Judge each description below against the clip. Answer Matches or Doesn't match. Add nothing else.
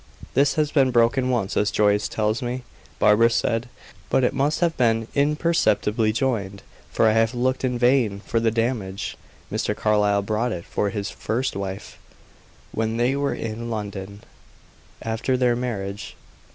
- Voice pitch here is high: Doesn't match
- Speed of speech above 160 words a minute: Doesn't match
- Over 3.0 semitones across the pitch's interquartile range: Matches